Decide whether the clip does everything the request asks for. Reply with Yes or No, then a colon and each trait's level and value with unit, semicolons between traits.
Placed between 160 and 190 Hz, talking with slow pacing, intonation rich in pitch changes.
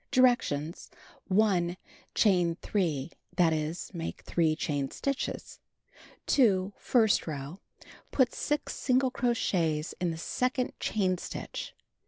Yes: medium, 185 Hz; slow, 105 wpm; wide, 6.7 semitones